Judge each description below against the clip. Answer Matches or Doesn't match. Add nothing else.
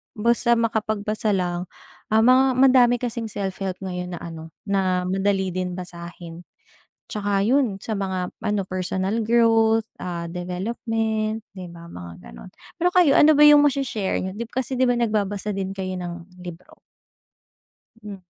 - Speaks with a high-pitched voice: Matches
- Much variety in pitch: Doesn't match